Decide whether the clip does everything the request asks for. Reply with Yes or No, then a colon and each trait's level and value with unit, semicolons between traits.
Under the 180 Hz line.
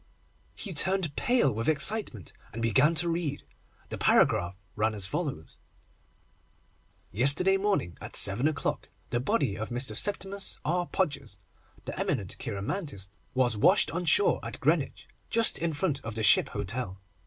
Yes: medium, 140 Hz